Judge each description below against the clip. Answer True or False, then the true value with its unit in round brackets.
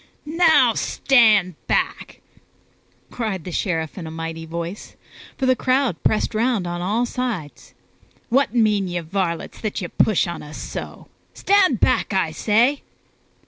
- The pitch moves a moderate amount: False (6.2 semitones)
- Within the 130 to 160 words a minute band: True (145 wpm)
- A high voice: True (205 Hz)